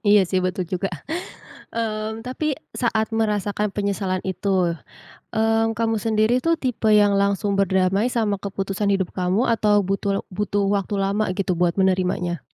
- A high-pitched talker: Yes, high, 200 Hz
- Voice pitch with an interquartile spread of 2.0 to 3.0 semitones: Yes, narrow, 2.4 semitones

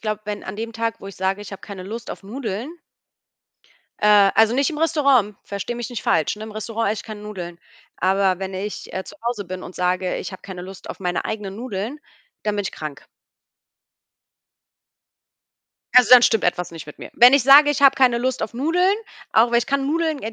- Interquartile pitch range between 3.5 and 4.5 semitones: Yes, average, 4.2 semitones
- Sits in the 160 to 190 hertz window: No, high, 215 Hz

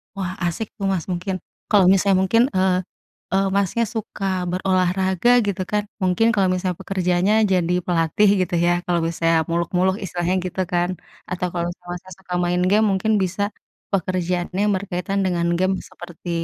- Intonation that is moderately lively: No, narrow, 1.7 semitones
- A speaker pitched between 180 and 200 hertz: Yes, medium, 185 Hz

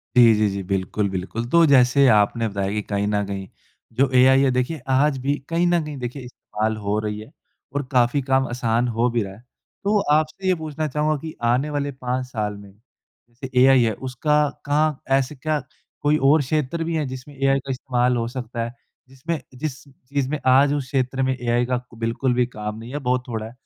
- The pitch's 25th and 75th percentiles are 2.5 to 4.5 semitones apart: Yes, average, 3.7 semitones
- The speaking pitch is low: Yes, low, 130 Hz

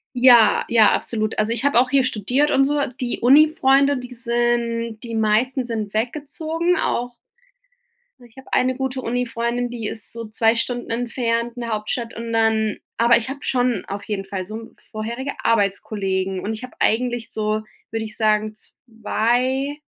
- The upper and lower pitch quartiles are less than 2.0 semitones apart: No, narrow, 2.6 semitones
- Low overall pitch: No, high, 235 Hz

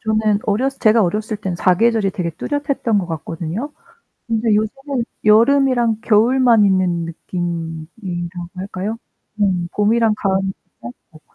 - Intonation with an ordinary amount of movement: Yes, average, 4.5 semitones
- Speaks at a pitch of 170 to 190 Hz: No, high, 210 Hz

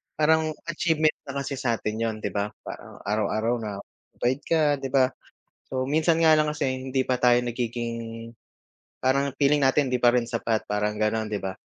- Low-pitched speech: Yes, low, 125 Hz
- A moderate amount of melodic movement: Yes, average, 4.0 semitones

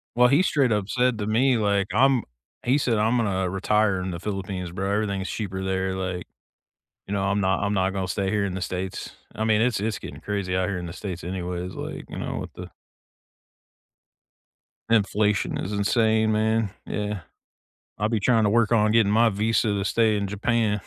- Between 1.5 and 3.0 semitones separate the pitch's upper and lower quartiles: Yes, narrow, 2.6 semitones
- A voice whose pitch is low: Yes, low, 105 Hz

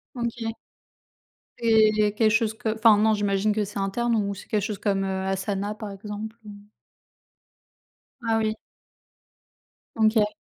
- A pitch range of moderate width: No, narrow, 1.5 semitones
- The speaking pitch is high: Yes, high, 215 Hz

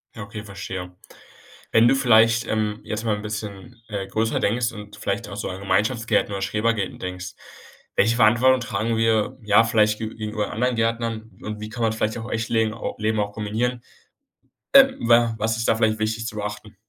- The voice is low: Yes, low, 110 Hz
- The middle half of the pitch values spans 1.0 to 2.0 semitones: Yes, narrow, 1.5 semitones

